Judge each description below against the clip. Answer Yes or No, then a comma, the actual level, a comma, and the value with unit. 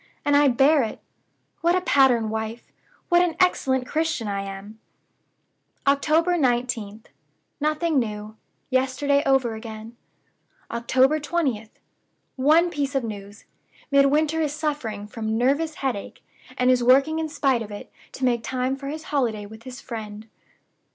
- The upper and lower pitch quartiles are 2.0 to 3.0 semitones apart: No, average, 4.9 semitones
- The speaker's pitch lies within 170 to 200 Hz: No, very high, 260 Hz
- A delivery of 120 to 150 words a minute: Yes, average, 140 wpm